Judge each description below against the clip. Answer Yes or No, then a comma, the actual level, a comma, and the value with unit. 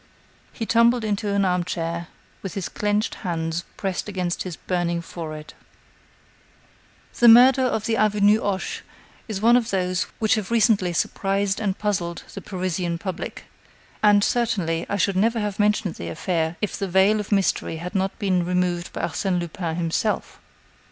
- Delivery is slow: No, average, 160 wpm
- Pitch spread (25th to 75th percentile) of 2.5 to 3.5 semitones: Yes, average, 3.2 semitones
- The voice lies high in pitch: Yes, high, 195 Hz